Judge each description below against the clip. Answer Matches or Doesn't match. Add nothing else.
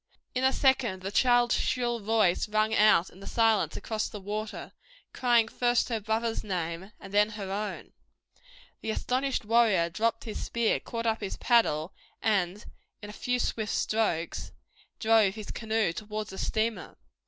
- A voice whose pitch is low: Doesn't match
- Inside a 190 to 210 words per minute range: Doesn't match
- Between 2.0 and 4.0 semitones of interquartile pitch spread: Matches